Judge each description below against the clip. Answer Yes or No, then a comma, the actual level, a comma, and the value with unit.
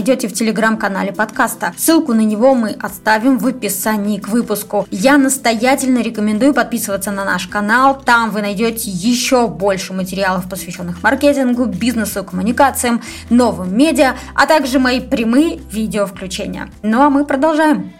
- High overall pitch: Yes, high, 230 Hz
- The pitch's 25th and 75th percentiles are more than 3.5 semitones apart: Yes, average, 4.2 semitones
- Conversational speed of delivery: Yes, average, 135 wpm